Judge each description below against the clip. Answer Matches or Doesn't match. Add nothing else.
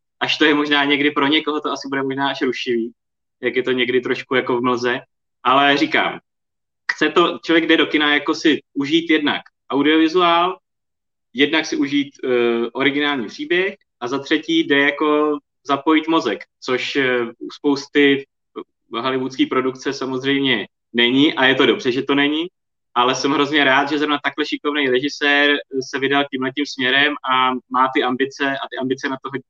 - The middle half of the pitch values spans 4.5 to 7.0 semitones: Doesn't match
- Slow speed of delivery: Doesn't match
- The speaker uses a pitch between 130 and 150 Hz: Matches